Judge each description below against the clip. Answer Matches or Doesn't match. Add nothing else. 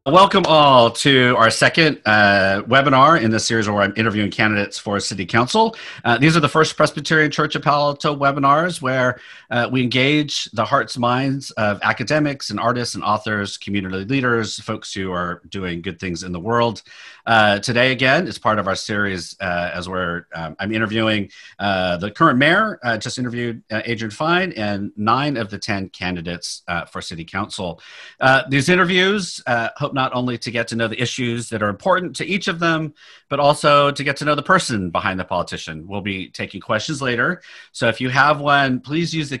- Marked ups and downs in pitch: Matches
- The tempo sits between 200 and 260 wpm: Matches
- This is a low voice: Matches